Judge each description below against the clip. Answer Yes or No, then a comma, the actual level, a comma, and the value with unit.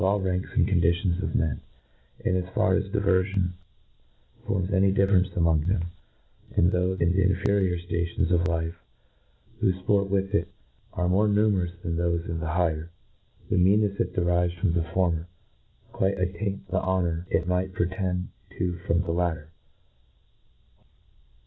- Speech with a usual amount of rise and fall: No, narrow, 2.1 semitones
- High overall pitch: No, very low, 90 Hz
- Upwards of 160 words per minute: Yes, average, 170 wpm